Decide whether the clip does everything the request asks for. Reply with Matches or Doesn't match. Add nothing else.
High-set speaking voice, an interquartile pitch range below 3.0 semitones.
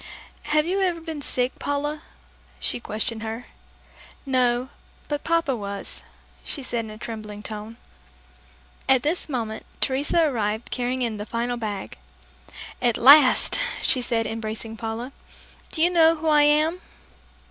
Doesn't match